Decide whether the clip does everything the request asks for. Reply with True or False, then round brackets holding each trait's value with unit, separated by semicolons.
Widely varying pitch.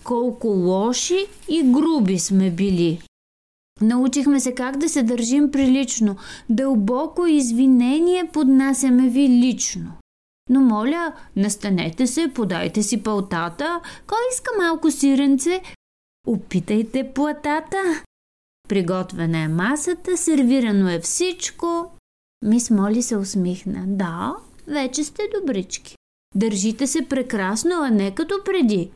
True (7.0 semitones)